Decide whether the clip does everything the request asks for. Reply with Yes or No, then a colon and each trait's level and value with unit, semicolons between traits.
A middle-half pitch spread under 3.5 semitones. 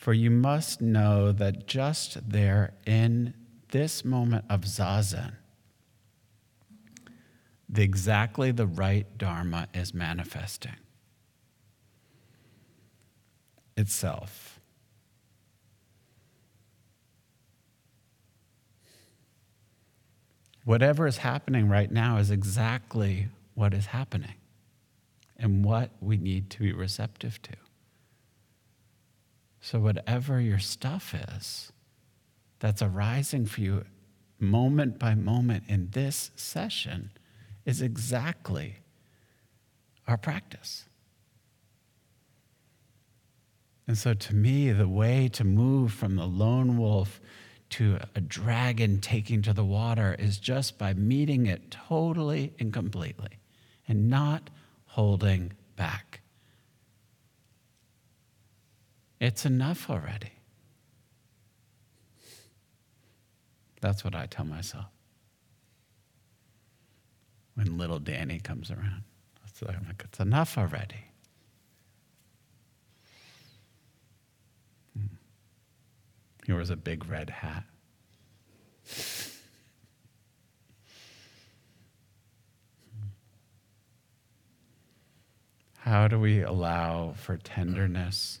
Yes: average, 2.8 semitones